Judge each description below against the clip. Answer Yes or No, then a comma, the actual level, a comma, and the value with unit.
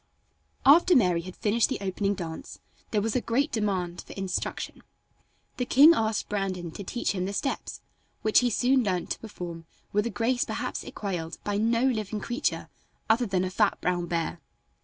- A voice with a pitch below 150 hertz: No, high, 205 Hz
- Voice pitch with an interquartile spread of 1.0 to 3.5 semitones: No, average, 4.5 semitones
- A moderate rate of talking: Yes, average, 180 wpm